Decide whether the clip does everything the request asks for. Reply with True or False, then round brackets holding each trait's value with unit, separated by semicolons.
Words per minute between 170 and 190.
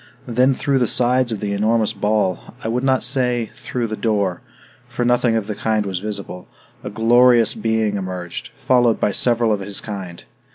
True (180 wpm)